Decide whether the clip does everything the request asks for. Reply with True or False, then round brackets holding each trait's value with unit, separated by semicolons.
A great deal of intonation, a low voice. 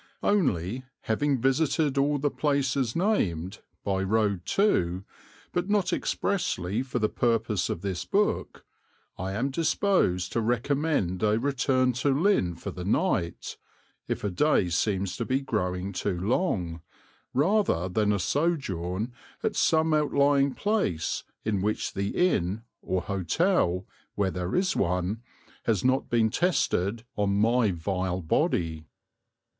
True (7.5 semitones; 110 Hz)